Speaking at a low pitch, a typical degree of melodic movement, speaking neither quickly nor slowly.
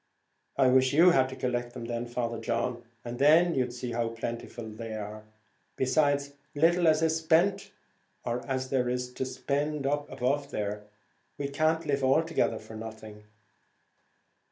Yes: low, 130 Hz; average, 3.8 semitones; average, 155 wpm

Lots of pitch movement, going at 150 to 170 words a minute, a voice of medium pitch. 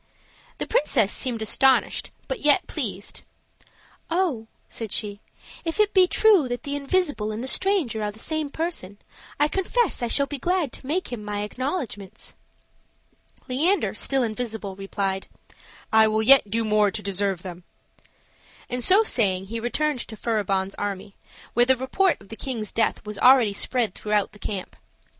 No: wide, 5.8 semitones; average, 160 wpm; high, 235 Hz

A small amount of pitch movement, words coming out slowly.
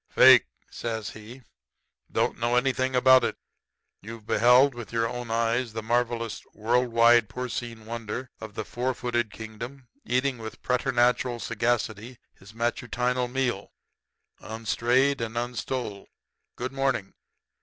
Yes: narrow, 1.8 semitones; slow, 125 wpm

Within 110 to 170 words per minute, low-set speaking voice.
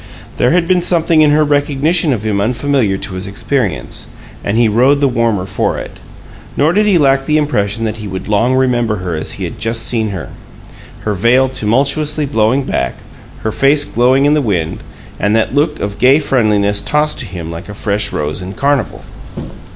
No: average, 195 wpm; low, 120 Hz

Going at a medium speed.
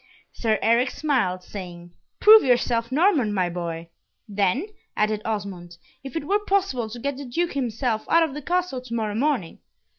Yes: average, 170 wpm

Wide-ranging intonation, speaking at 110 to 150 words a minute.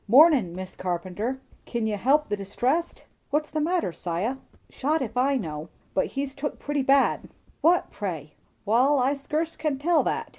No: wide, 6.8 semitones; average, 170 wpm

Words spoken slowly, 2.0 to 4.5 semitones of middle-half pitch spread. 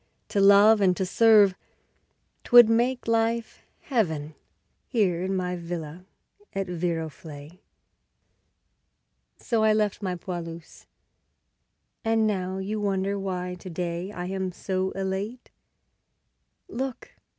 Yes: slow, 110 wpm; average, 3.3 semitones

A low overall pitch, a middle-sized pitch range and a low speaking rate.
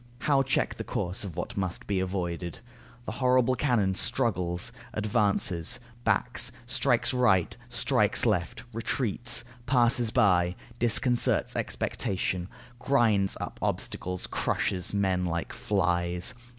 Yes: low, 100 Hz; average, 5.0 semitones; slow, 110 wpm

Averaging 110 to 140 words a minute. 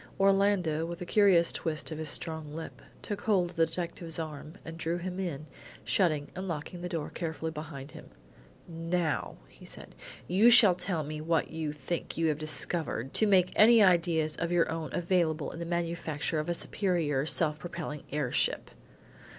No: average, 180 wpm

